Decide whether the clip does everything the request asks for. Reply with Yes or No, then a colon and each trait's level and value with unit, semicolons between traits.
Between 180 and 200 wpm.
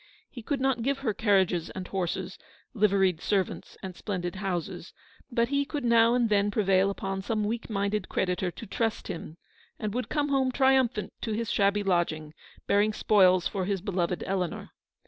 No: average, 170 wpm